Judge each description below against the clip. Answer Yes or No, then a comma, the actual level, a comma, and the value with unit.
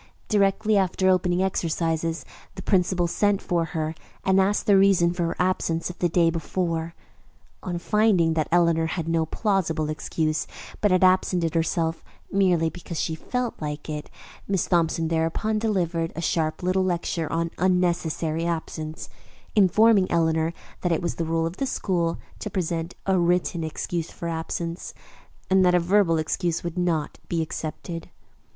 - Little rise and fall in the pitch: Yes, narrow, 2.3 semitones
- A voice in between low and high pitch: Yes, medium, 170 Hz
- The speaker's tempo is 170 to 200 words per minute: No, average, 160 wpm